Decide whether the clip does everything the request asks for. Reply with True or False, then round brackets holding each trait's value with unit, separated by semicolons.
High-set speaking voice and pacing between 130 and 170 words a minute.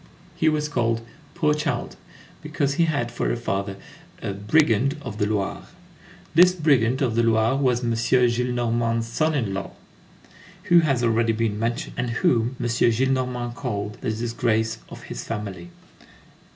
False (120 Hz; 150 wpm)